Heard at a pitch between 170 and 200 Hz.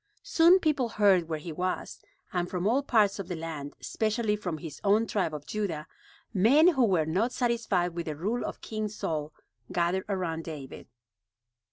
Yes: high, 190 Hz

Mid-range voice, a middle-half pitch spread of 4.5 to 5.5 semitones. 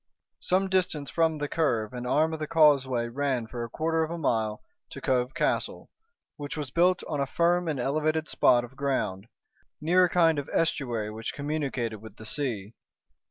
Yes: medium, 145 Hz; average, 4.9 semitones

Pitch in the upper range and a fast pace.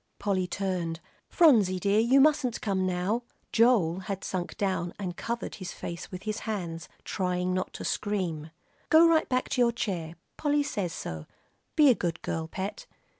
No: high, 195 Hz; average, 170 wpm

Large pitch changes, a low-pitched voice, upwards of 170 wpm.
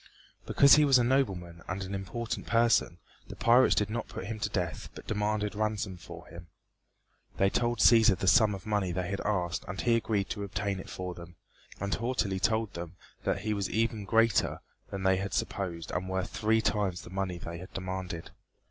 No: average, 3.1 semitones; low, 100 Hz; average, 200 wpm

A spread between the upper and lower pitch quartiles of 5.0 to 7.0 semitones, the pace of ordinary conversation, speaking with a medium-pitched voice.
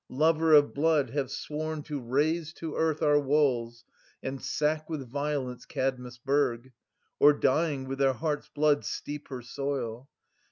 No: average, 2.7 semitones; average, 155 wpm; medium, 145 Hz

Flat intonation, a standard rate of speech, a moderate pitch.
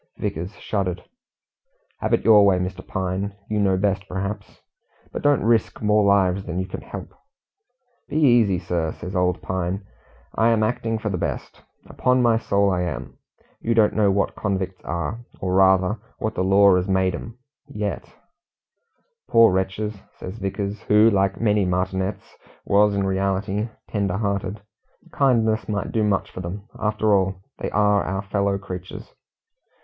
No: narrow, 2.2 semitones; average, 160 wpm; low, 100 Hz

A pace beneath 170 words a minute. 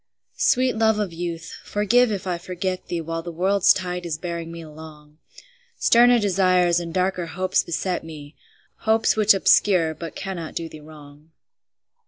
Yes: average, 160 wpm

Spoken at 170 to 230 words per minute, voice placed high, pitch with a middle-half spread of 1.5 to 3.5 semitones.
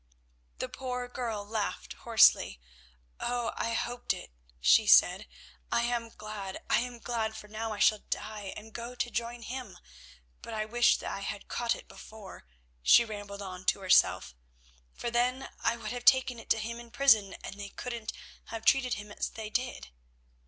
Yes: average, 180 wpm; high, 225 Hz; narrow, 2.5 semitones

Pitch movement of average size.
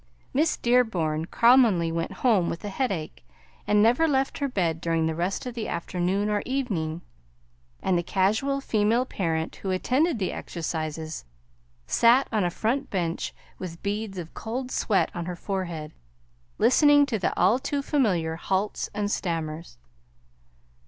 No: wide, 6.4 semitones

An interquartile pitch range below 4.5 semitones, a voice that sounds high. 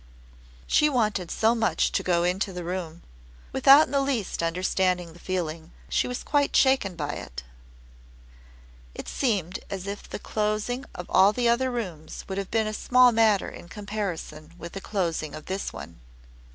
No: average, 5.0 semitones; high, 195 Hz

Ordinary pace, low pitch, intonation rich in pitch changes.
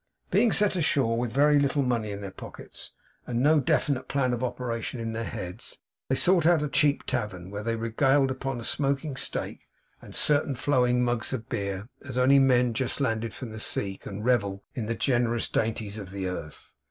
No: average, 195 wpm; low, 120 Hz; average, 3.8 semitones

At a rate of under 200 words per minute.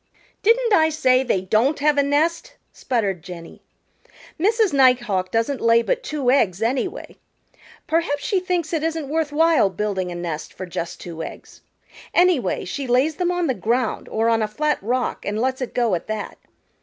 Yes: average, 180 wpm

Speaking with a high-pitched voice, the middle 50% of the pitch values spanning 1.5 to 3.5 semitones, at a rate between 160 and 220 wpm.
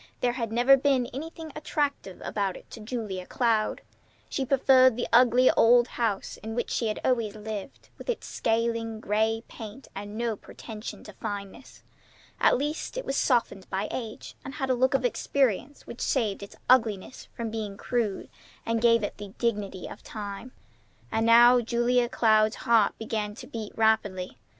Yes: high, 230 Hz; average, 2.9 semitones; average, 170 wpm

